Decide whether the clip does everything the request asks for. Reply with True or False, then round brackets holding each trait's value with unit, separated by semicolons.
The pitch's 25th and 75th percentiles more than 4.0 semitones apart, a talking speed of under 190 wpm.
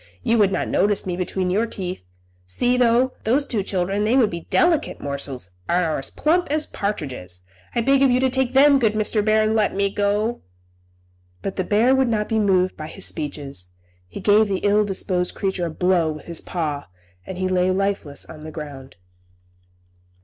False (4.8 semitones; 195 wpm)